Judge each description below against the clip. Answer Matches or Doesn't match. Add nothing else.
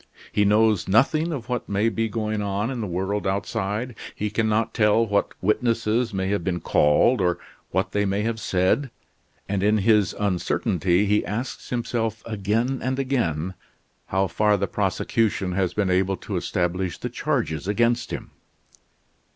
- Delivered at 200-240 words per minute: Doesn't match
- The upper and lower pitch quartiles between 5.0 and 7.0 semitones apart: Doesn't match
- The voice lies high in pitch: Doesn't match